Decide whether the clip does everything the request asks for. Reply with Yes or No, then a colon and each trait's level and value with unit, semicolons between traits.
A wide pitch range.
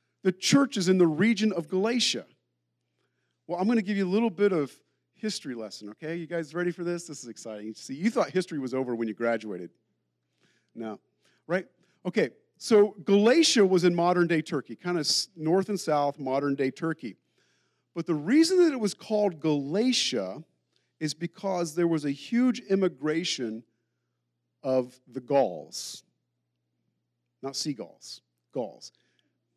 Yes: wide, 8.9 semitones